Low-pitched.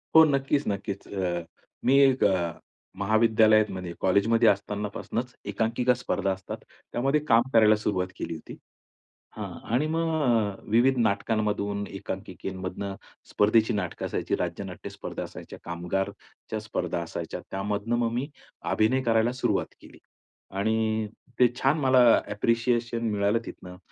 Yes: low, 110 Hz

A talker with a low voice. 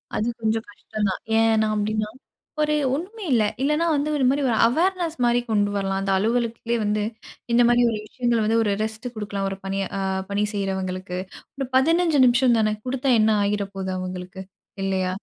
No: high, 220 Hz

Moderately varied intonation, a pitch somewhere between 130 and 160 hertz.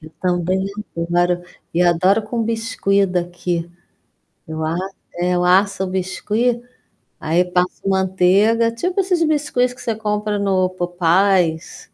No: average, 3.4 semitones; high, 190 Hz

